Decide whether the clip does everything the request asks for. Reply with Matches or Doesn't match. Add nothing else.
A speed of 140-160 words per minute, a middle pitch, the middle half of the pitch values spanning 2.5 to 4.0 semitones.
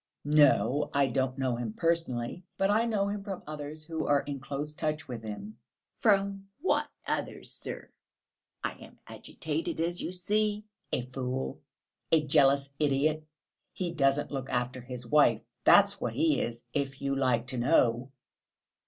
Doesn't match